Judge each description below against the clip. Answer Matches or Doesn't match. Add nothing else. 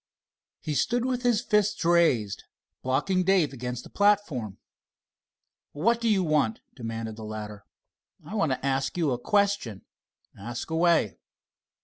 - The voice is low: Doesn't match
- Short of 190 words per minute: Matches